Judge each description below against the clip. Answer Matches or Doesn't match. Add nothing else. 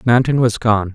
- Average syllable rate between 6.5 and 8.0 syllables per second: Doesn't match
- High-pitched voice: Doesn't match